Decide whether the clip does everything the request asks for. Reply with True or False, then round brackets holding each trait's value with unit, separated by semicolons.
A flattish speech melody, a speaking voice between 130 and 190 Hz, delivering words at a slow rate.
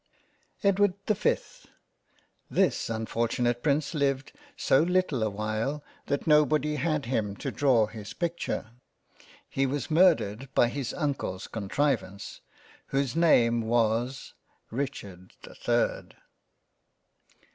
False (5.1 semitones; 135 Hz; 115 wpm)